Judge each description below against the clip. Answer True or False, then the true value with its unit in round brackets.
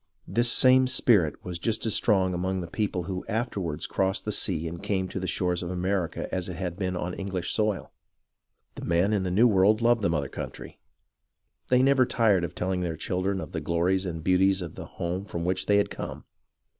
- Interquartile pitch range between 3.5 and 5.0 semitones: False (2.9 semitones)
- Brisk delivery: True (210 wpm)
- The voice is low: True (95 Hz)